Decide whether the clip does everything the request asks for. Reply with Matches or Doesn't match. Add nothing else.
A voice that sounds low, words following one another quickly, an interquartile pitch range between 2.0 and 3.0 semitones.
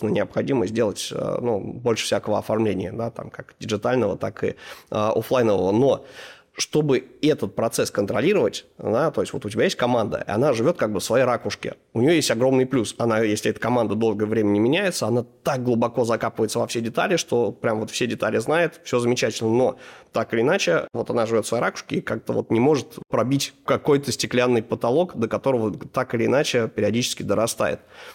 Matches